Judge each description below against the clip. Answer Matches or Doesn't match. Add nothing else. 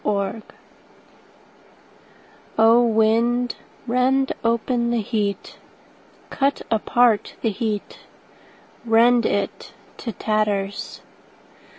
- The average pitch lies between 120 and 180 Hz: Doesn't match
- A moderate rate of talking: Doesn't match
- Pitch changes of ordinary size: Doesn't match